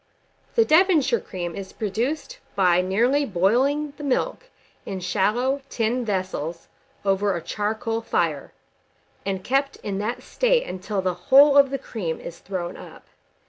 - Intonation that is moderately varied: No, wide, 6.6 semitones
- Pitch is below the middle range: No, high, 220 Hz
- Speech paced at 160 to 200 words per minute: No, average, 140 wpm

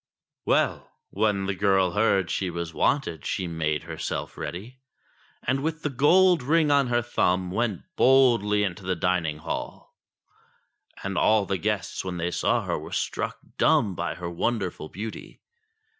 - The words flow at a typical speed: Yes, average, 155 wpm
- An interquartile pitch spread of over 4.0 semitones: Yes, average, 5.2 semitones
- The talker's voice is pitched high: No, low, 100 Hz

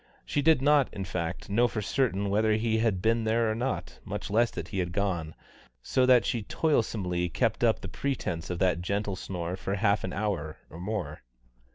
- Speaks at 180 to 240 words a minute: Yes, average, 200 wpm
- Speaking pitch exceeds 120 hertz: No, low, 105 Hz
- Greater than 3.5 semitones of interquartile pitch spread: Yes, average, 4.2 semitones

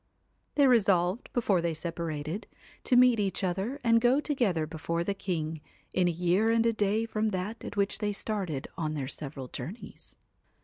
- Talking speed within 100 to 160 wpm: No, average, 175 wpm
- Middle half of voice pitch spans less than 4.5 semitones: No, average, 5.3 semitones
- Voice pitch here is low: No, high, 195 Hz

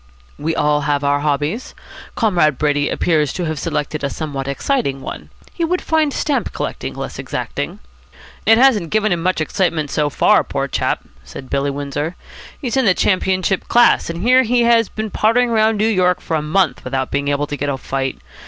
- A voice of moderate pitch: Yes, medium, 165 Hz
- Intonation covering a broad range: Yes, wide, 7.2 semitones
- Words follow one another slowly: No, average, 190 wpm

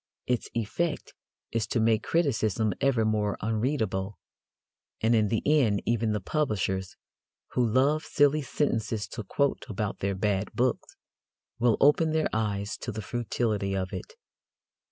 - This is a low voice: Yes, low, 110 Hz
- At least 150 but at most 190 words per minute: No, average, 140 wpm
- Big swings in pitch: No, average, 4.5 semitones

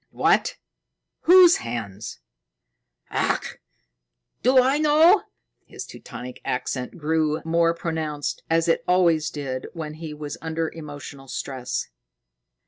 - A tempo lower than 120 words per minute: Yes, slow, 110 wpm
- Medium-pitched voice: Yes, medium, 160 Hz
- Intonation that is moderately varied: Yes, average, 3.2 semitones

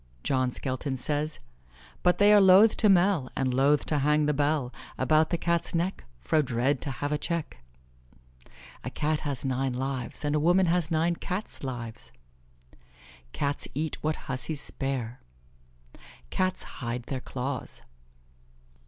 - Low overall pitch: No, medium, 145 Hz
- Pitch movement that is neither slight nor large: Yes, average, 4.2 semitones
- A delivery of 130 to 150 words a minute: Yes, average, 145 wpm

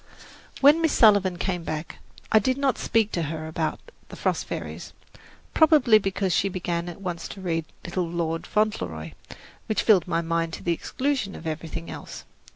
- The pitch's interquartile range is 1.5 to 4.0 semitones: No, average, 4.5 semitones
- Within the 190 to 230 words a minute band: No, average, 170 wpm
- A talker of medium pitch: Yes, medium, 180 Hz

